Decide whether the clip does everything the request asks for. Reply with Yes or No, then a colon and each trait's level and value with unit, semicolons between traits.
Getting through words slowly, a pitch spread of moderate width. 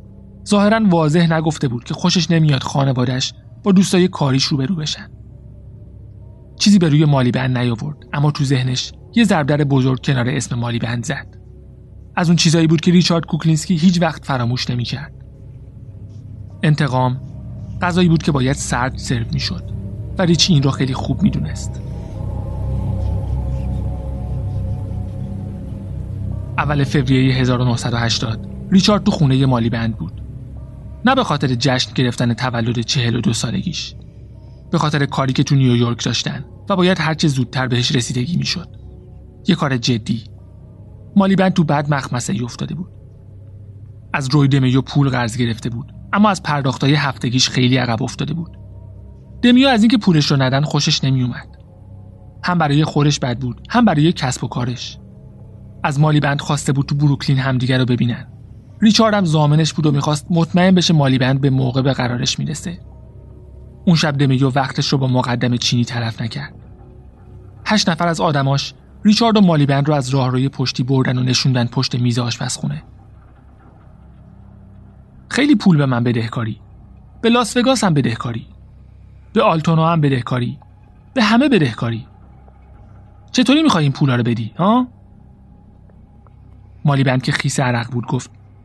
No: average, 150 wpm; average, 4.9 semitones